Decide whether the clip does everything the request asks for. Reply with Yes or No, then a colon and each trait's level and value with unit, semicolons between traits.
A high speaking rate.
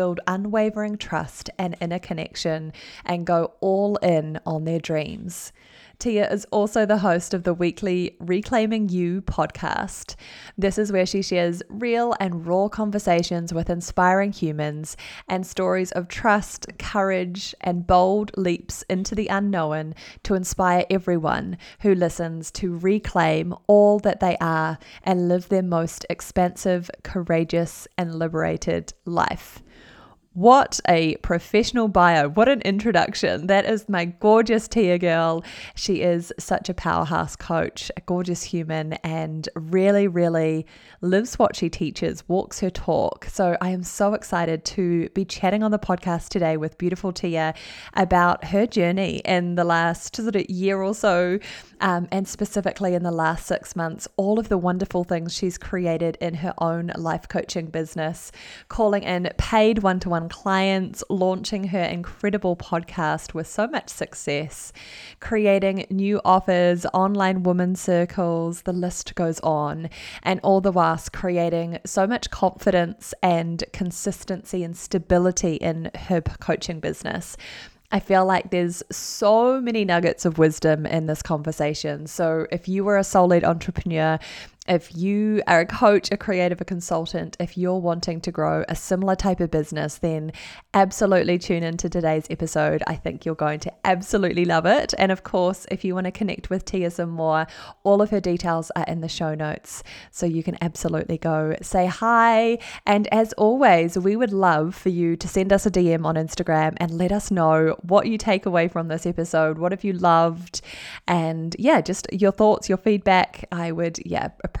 No: average, 160 wpm